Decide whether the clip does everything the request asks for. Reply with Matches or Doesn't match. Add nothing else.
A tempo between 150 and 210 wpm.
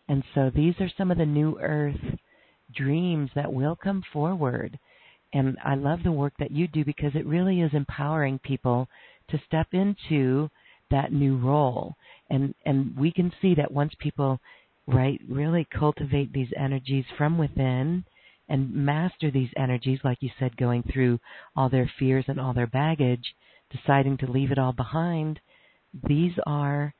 Matches